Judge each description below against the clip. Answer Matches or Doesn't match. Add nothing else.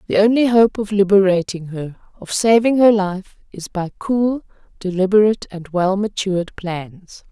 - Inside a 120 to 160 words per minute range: Matches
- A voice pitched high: Matches